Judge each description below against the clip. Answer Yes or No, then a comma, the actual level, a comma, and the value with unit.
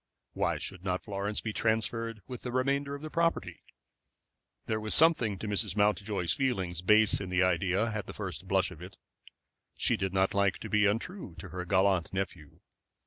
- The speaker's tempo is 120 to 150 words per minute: No, average, 185 wpm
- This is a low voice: Yes, low, 105 Hz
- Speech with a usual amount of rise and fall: Yes, average, 3.3 semitones